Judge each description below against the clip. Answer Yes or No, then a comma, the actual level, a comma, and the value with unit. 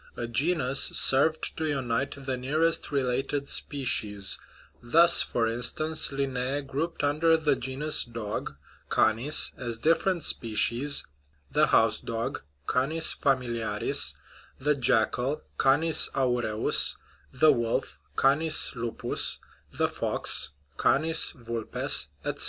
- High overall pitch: No, low, 135 Hz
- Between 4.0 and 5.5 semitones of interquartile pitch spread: Yes, average, 4.4 semitones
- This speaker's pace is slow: Yes, slow, 115 wpm